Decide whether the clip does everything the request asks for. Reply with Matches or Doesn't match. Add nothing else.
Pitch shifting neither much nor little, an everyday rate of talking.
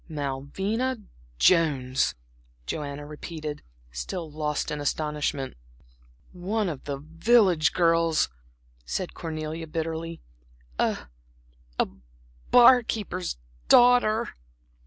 Doesn't match